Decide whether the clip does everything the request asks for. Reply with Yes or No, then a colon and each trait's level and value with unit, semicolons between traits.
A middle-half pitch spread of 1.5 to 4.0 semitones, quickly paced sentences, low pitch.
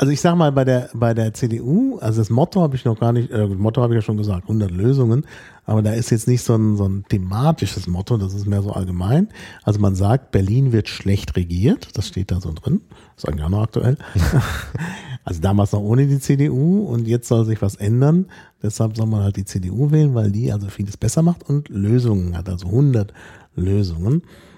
No: average, 4.8 semitones; fast, 220 wpm; low, 110 Hz